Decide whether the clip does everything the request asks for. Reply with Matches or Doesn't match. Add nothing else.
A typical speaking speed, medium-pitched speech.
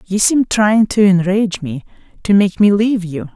Doesn't match